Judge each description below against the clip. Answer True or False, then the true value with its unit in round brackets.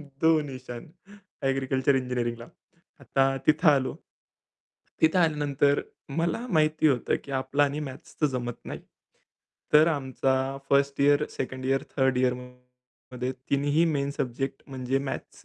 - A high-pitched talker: False (135 Hz)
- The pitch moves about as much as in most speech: False (2.2 semitones)